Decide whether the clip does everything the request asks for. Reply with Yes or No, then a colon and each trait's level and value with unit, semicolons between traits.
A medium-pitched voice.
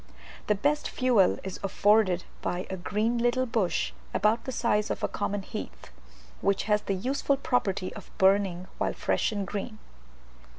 No: high, 205 Hz